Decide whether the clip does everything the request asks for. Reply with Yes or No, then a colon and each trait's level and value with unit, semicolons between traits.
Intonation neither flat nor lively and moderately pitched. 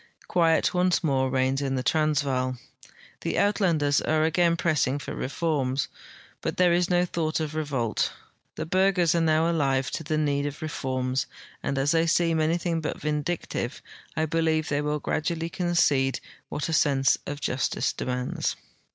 Yes: average, 3.5 semitones; medium, 155 Hz